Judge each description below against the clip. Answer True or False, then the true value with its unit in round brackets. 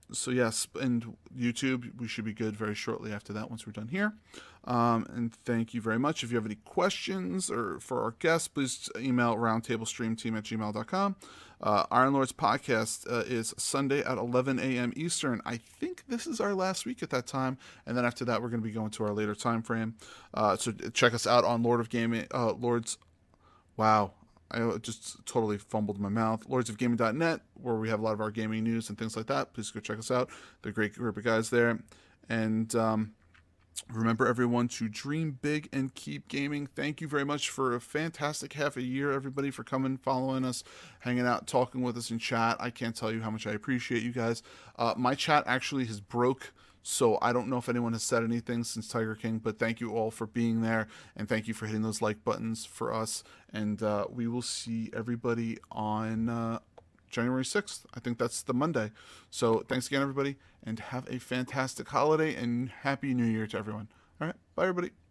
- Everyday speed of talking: False (210 wpm)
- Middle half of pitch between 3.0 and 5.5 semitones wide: False (2.5 semitones)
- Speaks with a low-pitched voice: True (120 Hz)